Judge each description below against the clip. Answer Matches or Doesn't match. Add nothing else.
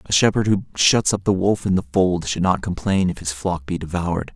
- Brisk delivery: Matches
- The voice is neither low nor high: Doesn't match